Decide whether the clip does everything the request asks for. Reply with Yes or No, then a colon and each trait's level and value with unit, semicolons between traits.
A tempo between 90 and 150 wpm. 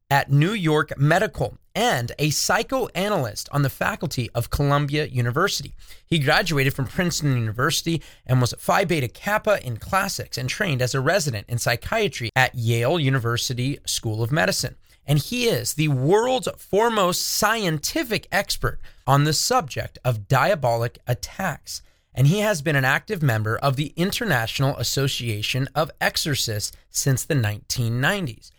Yes: average, 145 wpm